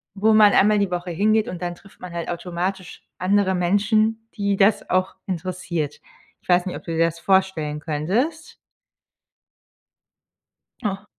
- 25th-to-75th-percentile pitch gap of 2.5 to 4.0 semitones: Yes, average, 2.8 semitones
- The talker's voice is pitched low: No, medium, 185 Hz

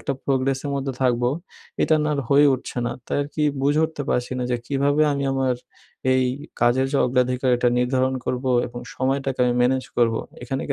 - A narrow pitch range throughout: Yes, narrow, 2.0 semitones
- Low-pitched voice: Yes, low, 130 Hz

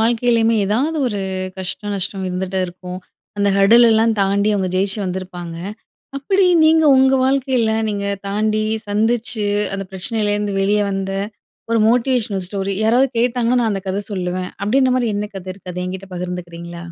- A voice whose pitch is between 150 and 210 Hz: Yes, high, 205 Hz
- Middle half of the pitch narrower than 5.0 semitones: Yes, average, 3.7 semitones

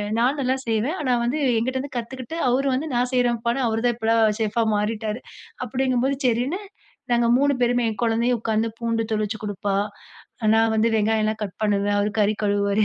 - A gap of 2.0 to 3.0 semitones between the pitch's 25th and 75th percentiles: Yes, narrow, 2.6 semitones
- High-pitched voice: Yes, high, 230 Hz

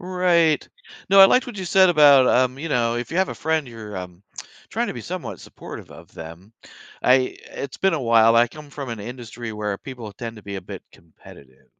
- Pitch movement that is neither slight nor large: No, wide, 6.7 semitones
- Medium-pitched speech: No, low, 125 Hz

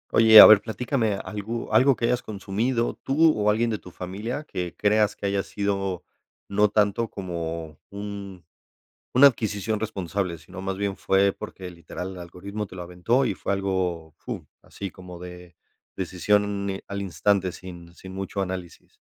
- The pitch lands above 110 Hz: No, low, 100 Hz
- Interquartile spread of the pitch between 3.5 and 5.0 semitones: No, average, 2.9 semitones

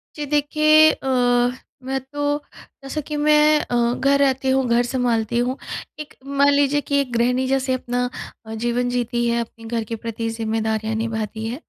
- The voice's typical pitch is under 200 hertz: No, very high, 250 Hz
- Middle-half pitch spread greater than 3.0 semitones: Yes, average, 3.5 semitones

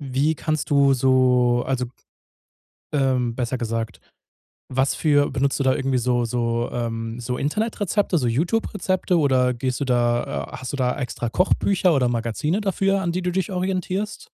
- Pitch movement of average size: No, wide, 6.0 semitones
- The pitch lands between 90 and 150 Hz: Yes, low, 135 Hz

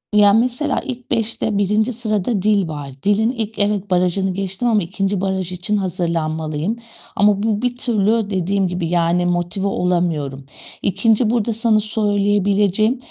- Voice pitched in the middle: No, high, 200 Hz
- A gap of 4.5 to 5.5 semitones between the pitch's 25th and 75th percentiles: No, average, 3.4 semitones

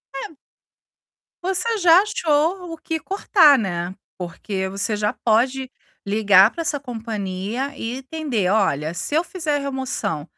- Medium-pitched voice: No, very high, 255 Hz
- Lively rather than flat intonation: Yes, wide, 8.1 semitones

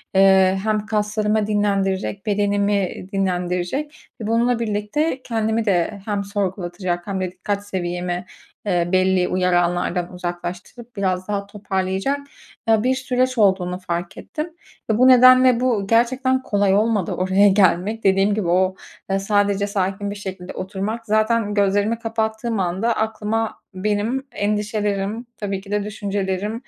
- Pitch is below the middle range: No, high, 205 Hz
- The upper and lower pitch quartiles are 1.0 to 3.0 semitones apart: Yes, average, 2.7 semitones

